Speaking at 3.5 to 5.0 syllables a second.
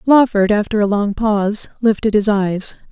Yes: 4.7 syllables/s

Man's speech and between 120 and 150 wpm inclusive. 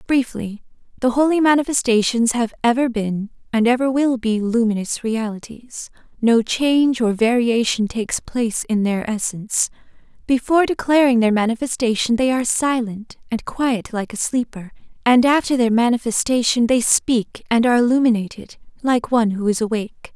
No: female; average, 145 wpm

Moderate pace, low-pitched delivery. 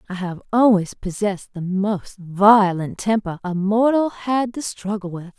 No: average, 155 wpm; high, 200 Hz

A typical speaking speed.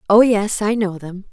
No: fast, 225 wpm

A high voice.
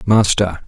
No: low, 100 Hz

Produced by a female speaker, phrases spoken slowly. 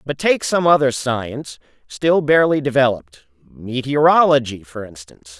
No: male; slow, 120 wpm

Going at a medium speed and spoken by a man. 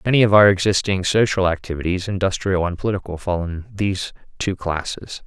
Yes: average, 160 wpm; male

